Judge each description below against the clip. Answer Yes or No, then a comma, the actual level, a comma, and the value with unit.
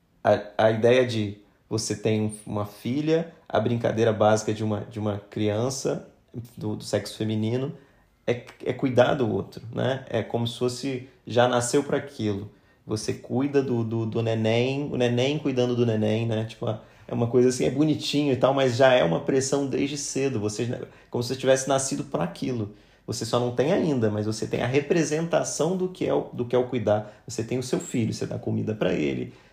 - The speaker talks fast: Yes, fast, 200 wpm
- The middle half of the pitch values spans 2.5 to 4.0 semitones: Yes, average, 3.7 semitones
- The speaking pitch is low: Yes, low, 120 Hz